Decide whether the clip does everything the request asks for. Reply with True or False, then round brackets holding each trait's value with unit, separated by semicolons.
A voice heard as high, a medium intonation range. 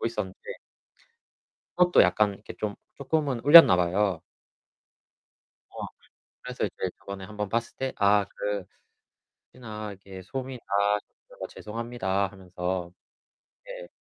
False (105 Hz; 4.0 semitones)